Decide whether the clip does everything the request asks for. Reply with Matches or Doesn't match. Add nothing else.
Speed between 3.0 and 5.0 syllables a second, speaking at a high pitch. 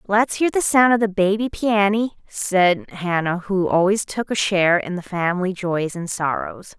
Matches